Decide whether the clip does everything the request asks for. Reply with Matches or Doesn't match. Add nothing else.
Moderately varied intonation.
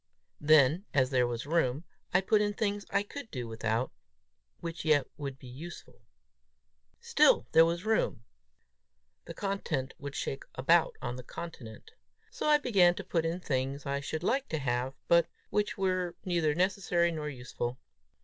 Doesn't match